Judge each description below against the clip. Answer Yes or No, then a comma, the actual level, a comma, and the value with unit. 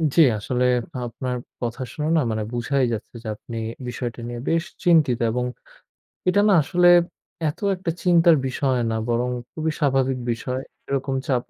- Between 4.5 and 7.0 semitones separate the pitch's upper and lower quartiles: Yes, average, 4.8 semitones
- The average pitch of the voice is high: No, low, 130 Hz